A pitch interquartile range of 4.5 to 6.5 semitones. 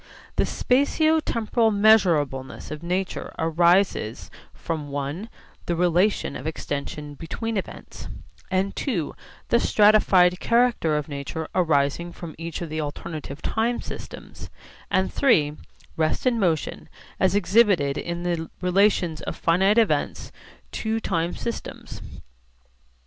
Yes: average, 5.2 semitones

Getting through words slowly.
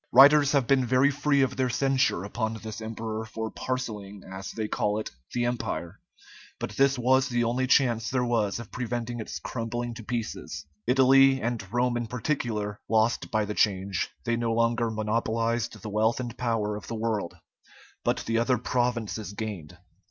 No: average, 175 wpm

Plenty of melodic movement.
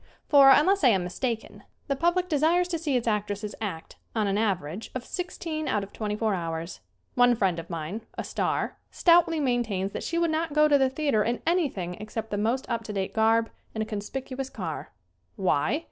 Yes: wide, 6.6 semitones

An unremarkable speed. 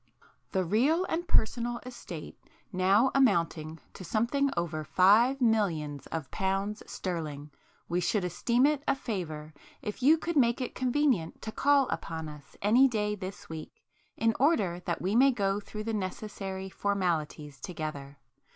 Yes: average, 150 wpm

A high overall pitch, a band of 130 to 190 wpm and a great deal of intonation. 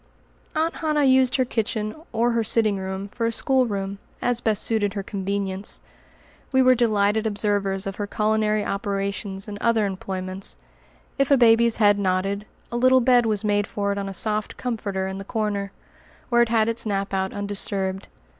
No: high, 210 Hz; average, 175 wpm; average, 2.8 semitones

